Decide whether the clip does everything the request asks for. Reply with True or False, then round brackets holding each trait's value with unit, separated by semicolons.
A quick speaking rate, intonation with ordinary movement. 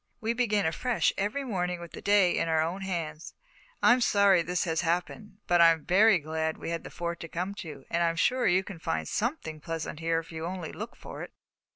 True (225 wpm; 3.7 semitones)